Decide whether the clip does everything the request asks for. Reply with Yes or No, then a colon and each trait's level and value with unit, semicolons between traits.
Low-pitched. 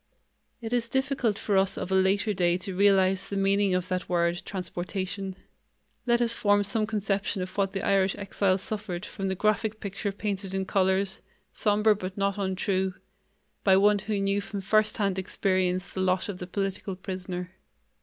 No: high, 195 Hz